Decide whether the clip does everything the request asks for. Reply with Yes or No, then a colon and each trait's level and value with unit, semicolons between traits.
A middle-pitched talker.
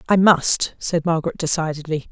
Yes: medium, 165 Hz